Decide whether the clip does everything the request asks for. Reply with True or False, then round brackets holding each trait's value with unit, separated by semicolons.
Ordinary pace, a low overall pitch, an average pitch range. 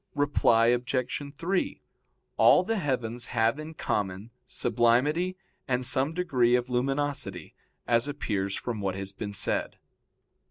False (125 wpm; 125 Hz; 4.3 semitones)